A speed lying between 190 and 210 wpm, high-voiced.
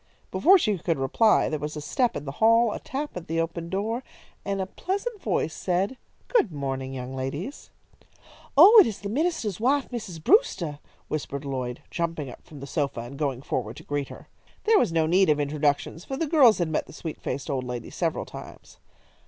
No: average, 200 wpm; medium, 165 Hz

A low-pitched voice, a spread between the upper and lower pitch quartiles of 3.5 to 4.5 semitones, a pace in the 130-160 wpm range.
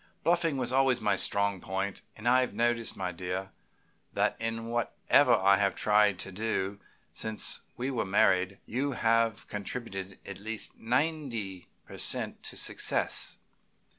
Yes: low, 110 Hz; average, 3.8 semitones; average, 145 wpm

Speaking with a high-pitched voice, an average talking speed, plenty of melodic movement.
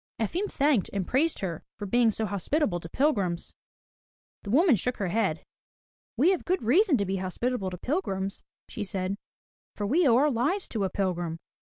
Yes: high, 215 Hz; average, 180 wpm; wide, 7.0 semitones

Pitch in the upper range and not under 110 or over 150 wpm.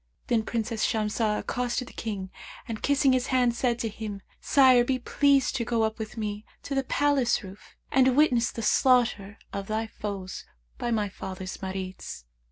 No: high, 230 Hz; average, 175 wpm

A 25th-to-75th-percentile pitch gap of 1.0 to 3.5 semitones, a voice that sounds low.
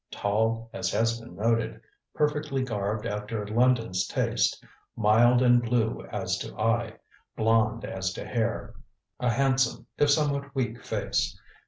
Yes: narrow, 2.4 semitones; low, 115 Hz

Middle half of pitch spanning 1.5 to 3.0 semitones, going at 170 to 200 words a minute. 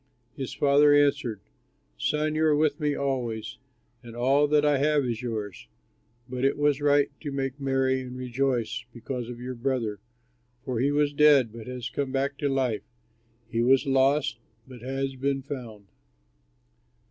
No: average, 2.7 semitones; average, 160 wpm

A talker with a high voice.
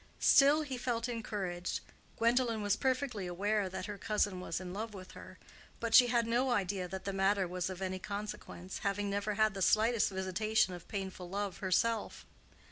Yes: high, 205 Hz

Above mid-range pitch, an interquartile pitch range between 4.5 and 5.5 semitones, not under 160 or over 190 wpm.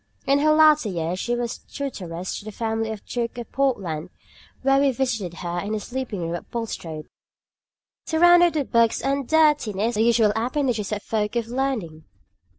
Yes: high, 230 Hz; average, 5.2 semitones; average, 175 wpm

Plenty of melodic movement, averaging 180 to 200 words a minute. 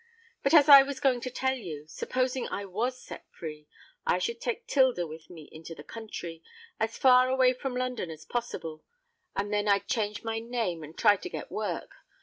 Yes: wide, 7.2 semitones; average, 185 wpm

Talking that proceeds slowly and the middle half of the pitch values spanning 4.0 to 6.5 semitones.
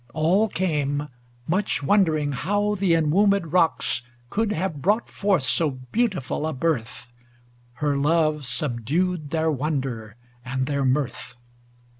Yes: slow, 125 wpm; average, 5.1 semitones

